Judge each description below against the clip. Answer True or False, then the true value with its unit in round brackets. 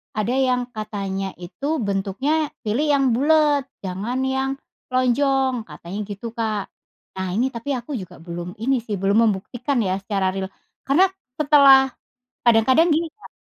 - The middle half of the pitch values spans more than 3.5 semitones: True (5.6 semitones)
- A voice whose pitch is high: True (240 Hz)